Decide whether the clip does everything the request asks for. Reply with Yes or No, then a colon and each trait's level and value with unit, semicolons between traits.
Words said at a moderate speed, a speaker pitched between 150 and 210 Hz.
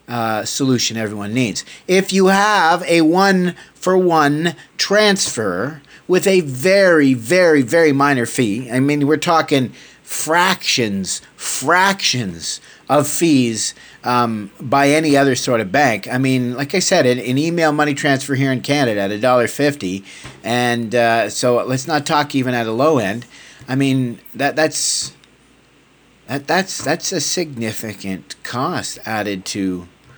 No: average, 145 wpm; medium, 140 Hz